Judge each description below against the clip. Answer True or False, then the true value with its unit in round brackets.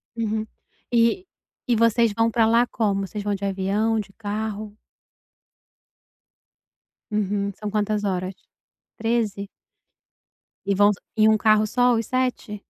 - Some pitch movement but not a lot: False (1.9 semitones)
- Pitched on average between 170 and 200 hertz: False (215 Hz)